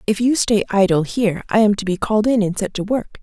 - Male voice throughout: No, female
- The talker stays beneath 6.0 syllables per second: No, 6.1 syllables/s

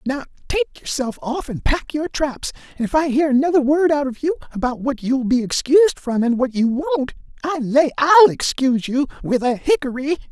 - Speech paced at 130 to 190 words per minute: No, average, 200 wpm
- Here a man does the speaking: Yes, male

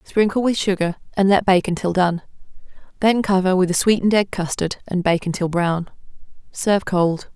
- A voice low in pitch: No, medium, 185 Hz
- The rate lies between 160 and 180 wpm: Yes, average, 170 wpm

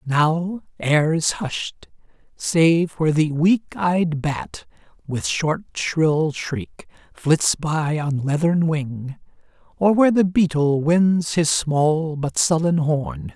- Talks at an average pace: No, slow, 130 wpm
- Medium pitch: Yes, medium, 160 Hz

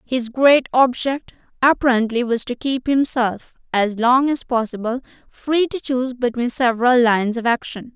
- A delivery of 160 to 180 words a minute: No, average, 150 wpm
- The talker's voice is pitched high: Yes, very high, 250 Hz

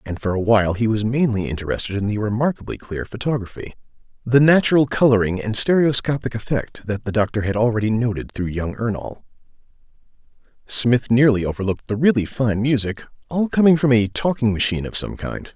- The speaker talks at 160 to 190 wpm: Yes, average, 170 wpm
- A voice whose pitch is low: Yes, low, 115 Hz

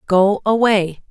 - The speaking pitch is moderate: No, high, 200 Hz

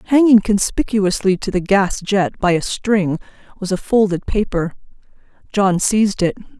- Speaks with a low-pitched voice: No, high, 195 Hz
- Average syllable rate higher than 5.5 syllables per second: No, 4.8 syllables/s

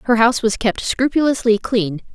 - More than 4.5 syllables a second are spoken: Yes, 5.0 syllables/s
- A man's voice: No, female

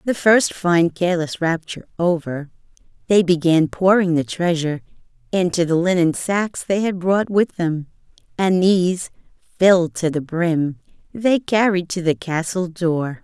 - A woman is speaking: Yes, female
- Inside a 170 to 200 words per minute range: No, average, 145 wpm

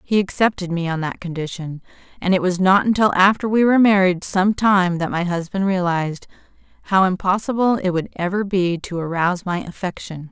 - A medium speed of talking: Yes, average, 180 wpm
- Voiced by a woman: Yes, female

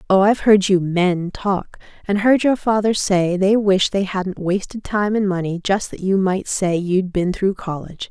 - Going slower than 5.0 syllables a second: Yes, 4.5 syllables/s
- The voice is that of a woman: Yes, female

